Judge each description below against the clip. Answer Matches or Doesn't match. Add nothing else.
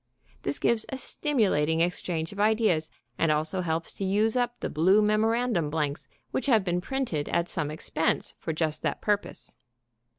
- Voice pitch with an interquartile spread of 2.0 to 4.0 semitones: Doesn't match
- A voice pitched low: Doesn't match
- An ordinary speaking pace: Matches